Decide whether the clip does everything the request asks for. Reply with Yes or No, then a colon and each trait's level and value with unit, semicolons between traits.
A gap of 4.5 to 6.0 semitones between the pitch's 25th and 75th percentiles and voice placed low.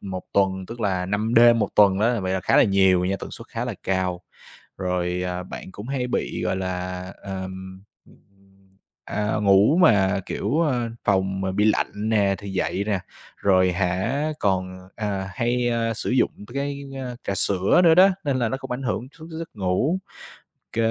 No: average, 4.1 semitones; low, 100 Hz